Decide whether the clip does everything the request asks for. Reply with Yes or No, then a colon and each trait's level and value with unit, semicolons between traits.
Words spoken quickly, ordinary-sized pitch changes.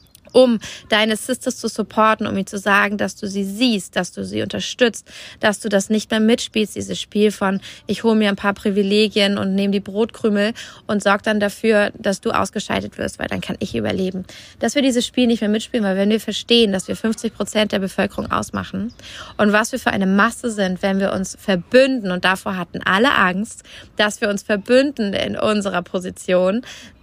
No: fast, 200 wpm; narrow, 2.3 semitones